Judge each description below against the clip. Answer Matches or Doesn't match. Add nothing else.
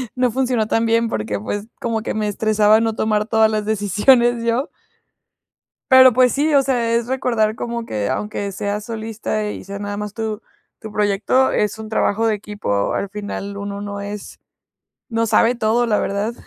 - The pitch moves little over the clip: Matches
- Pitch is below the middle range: Doesn't match